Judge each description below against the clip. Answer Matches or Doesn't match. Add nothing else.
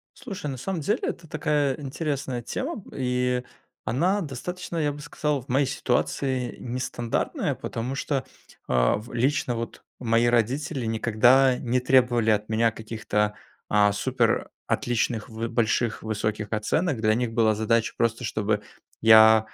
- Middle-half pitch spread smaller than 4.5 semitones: Matches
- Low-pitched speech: Matches